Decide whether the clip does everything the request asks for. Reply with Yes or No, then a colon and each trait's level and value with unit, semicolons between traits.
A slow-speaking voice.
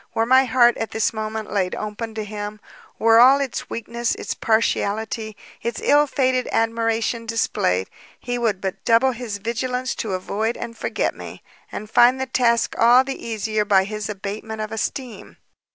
No: average, 170 wpm